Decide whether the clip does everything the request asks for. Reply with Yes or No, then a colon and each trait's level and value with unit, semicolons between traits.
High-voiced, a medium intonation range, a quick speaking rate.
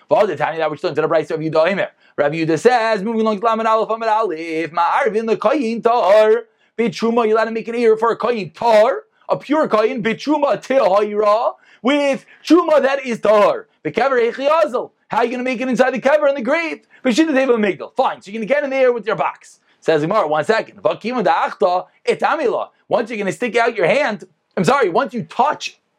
Yes: high, 225 Hz; average, 4.4 semitones; fast, 235 wpm